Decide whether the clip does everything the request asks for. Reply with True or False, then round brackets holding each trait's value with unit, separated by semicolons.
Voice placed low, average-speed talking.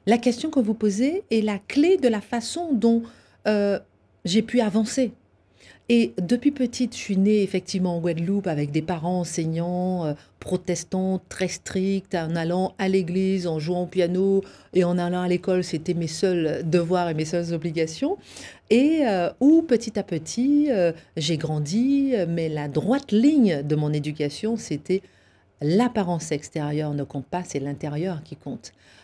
False (185 Hz; 165 wpm)